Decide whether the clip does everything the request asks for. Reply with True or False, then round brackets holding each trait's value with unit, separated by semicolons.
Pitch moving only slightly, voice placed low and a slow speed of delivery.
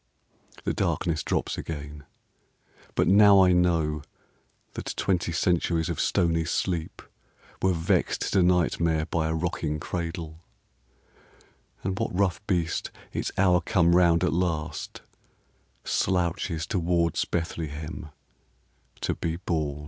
True (2.0 semitones; 85 Hz; 115 wpm)